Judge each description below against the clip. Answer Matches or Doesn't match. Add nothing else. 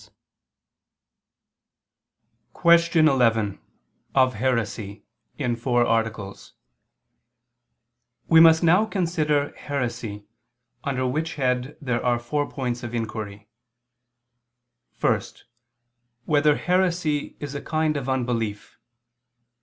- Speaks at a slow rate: Matches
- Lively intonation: Doesn't match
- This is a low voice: Matches